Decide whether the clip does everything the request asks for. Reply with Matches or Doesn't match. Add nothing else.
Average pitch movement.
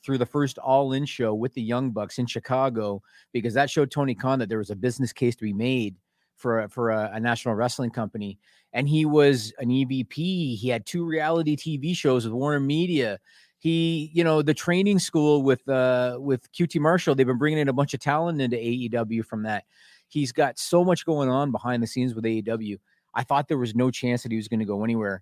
Matches